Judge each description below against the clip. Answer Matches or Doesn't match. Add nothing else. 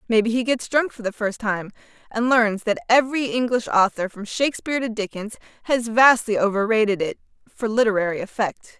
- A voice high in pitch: Matches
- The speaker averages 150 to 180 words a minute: Matches